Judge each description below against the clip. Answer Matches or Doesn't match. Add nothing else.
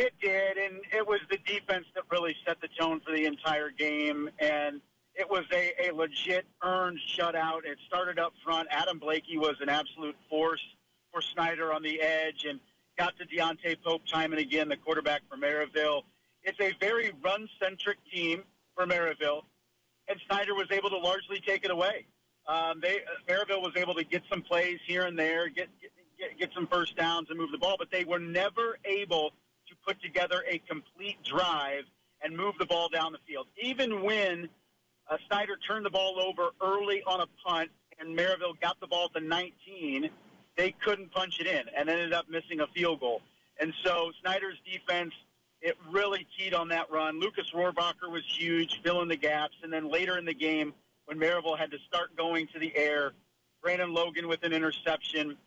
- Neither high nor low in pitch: Matches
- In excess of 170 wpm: Matches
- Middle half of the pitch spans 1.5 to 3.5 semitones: Matches